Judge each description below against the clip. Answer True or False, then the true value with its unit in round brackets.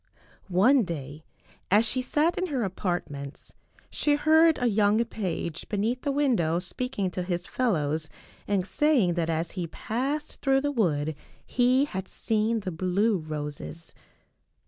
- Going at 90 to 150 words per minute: True (145 wpm)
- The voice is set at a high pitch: True (205 Hz)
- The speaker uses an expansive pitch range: True (7.2 semitones)